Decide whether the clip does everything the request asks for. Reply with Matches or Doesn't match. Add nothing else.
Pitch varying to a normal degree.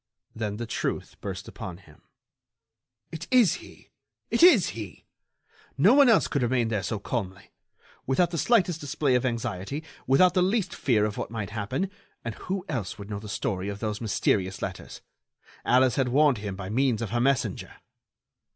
Doesn't match